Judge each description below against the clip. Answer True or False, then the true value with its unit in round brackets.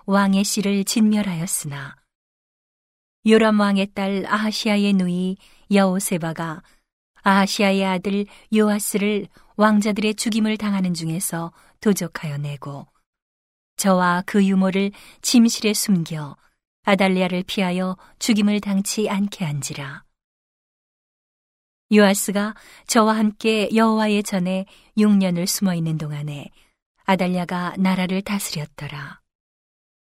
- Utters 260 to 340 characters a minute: False (240 characters per minute)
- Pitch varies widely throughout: False (2.7 semitones)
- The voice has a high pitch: True (195 Hz)